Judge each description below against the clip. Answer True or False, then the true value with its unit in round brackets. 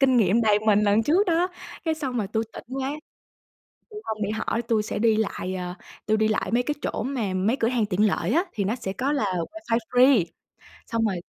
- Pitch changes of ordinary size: True (4.0 semitones)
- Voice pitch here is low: False (225 Hz)